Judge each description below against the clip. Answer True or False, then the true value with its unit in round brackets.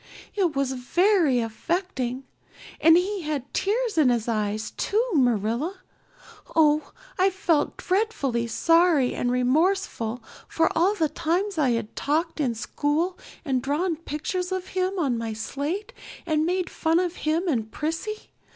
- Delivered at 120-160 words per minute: True (140 wpm)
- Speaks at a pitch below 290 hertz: False (315 Hz)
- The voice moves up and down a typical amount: False (6.5 semitones)